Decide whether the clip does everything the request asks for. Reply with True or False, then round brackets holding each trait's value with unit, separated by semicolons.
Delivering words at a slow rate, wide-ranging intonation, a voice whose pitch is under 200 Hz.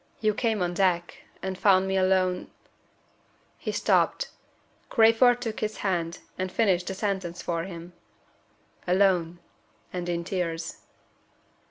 False (130 wpm; 2.9 semitones; 185 Hz)